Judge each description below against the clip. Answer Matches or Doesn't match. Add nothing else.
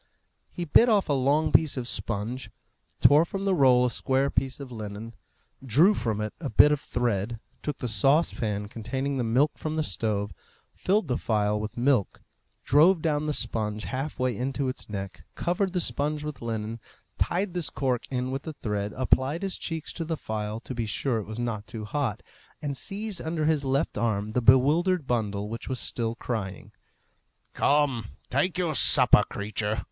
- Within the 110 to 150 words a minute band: Doesn't match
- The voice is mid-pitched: Doesn't match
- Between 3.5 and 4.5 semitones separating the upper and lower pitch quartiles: Doesn't match